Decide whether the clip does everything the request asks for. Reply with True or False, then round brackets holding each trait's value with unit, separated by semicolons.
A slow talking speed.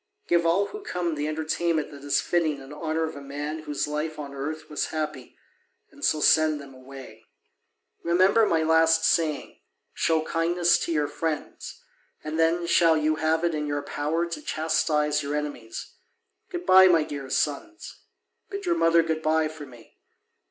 False (175 wpm)